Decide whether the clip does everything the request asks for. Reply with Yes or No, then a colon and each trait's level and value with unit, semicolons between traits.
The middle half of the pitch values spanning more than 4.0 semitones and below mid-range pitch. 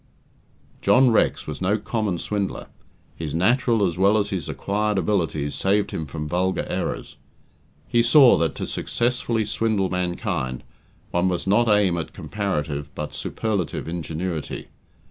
Yes: average, 4.5 semitones; very low, 95 Hz